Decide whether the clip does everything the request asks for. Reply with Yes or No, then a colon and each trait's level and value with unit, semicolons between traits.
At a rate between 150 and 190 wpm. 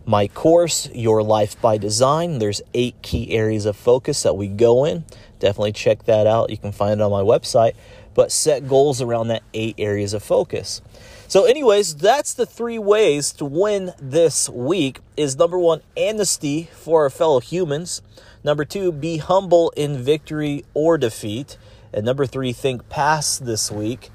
Yes: average, 170 wpm